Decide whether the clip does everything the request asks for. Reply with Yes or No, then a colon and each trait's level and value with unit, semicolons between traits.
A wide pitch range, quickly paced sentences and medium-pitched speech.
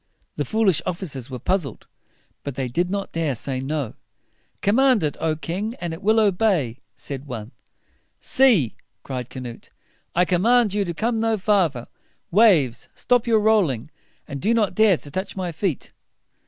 No: wide, 7.5 semitones; average, 165 wpm; medium, 180 Hz